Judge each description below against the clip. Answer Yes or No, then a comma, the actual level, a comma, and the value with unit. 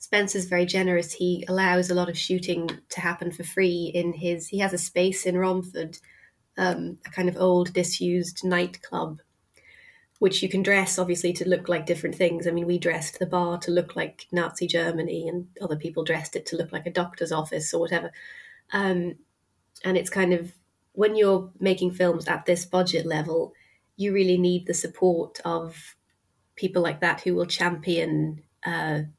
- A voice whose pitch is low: No, medium, 175 Hz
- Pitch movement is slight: Yes, narrow, 1.5 semitones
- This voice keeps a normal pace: Yes, average, 180 wpm